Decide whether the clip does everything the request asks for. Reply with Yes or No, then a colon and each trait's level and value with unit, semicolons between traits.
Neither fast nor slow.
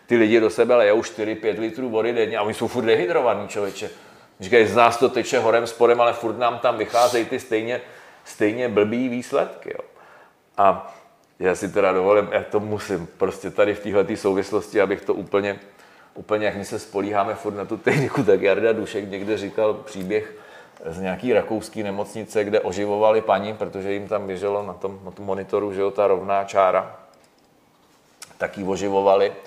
No: fast, 180 wpm